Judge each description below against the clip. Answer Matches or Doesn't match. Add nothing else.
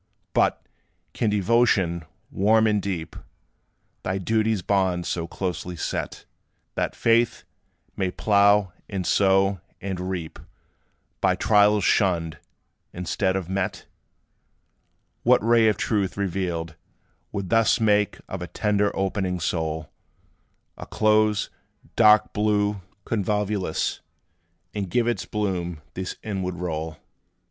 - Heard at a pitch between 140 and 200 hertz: Doesn't match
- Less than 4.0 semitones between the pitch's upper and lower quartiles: Matches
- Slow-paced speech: Matches